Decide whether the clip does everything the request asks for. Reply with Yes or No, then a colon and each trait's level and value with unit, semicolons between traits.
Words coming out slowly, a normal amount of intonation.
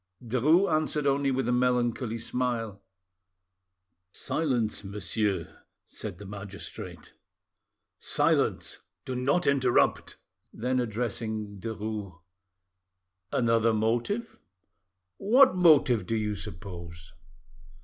Yes: slow, 85 wpm; average, 4.0 semitones